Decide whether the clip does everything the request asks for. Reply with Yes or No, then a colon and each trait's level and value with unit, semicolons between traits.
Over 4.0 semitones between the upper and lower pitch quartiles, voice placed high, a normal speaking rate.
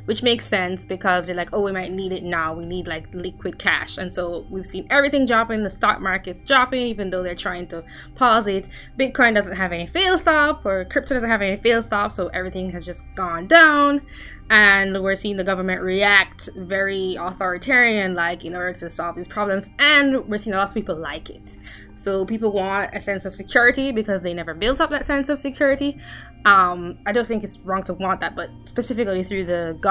No: average, 4.7 semitones; high, 195 Hz; fast, 215 wpm